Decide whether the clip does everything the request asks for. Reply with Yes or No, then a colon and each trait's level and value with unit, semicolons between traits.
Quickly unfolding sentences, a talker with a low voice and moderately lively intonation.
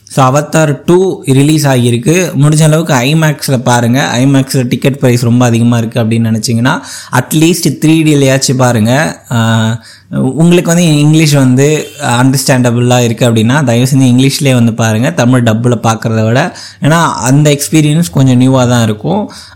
Yes: fast, 140 wpm; low, 130 Hz; average, 4.1 semitones